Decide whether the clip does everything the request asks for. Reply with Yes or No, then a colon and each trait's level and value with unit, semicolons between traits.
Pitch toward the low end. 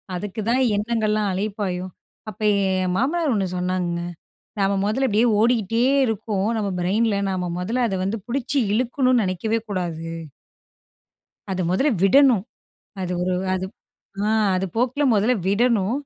No: high, 210 Hz